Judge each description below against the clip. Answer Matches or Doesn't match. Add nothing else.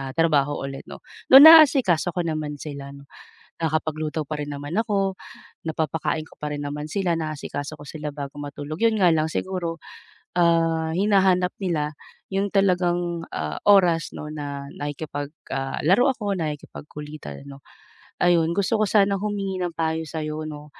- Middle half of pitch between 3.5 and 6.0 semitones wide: Matches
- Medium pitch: Matches